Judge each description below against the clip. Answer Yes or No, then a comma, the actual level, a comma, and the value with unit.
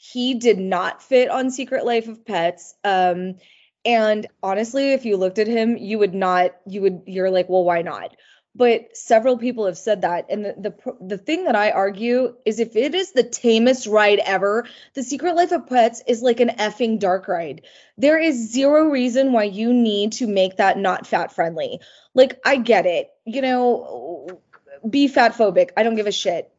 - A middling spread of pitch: Yes, average, 4.2 semitones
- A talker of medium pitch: No, high, 225 Hz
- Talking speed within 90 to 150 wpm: No, average, 195 wpm